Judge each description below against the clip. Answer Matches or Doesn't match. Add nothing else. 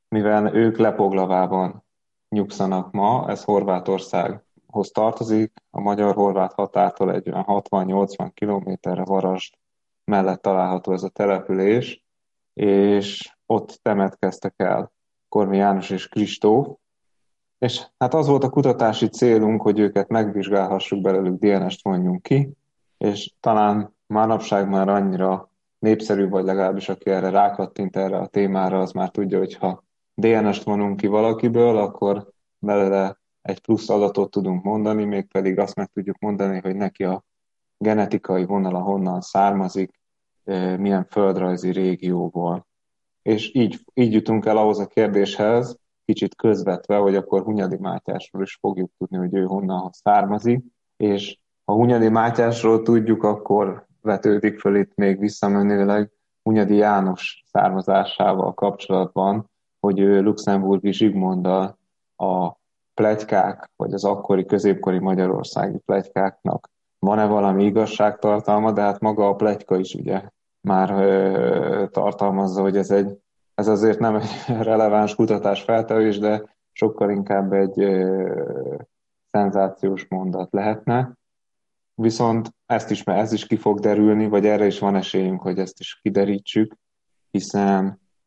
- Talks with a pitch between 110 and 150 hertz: Doesn't match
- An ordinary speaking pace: Matches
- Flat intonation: Matches